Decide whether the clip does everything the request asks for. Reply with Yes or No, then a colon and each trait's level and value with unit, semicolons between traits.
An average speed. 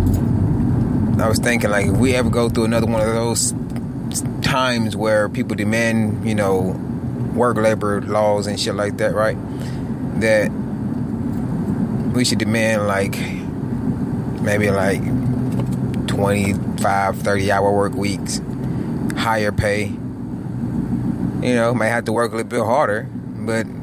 No: slow, 130 wpm